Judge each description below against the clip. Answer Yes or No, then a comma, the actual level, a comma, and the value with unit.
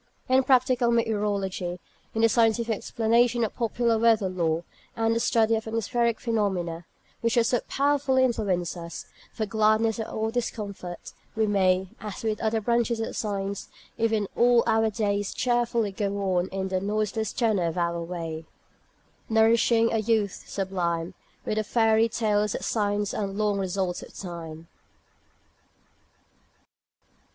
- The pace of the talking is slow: No, average, 145 wpm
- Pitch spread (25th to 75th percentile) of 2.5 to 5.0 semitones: Yes, average, 3.0 semitones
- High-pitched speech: Yes, high, 215 Hz